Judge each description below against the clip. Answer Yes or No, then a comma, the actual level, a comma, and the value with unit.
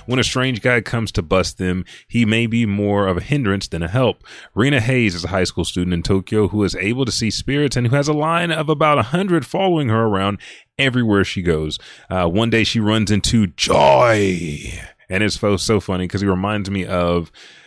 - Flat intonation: No, average, 4.9 semitones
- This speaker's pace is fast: Yes, fast, 220 wpm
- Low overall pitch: Yes, low, 105 Hz